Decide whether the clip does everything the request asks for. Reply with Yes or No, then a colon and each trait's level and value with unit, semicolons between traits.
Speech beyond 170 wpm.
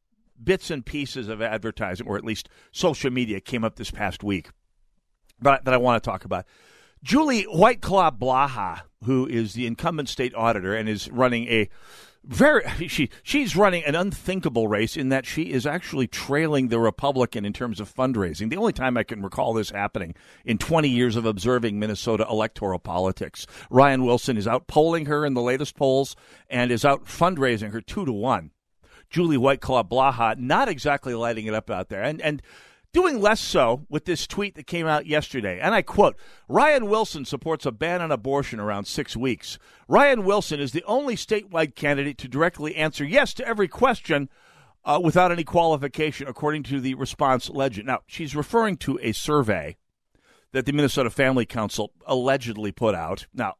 Yes: average, 180 wpm